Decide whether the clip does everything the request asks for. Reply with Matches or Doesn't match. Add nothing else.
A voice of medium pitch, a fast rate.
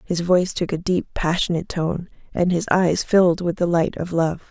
Matches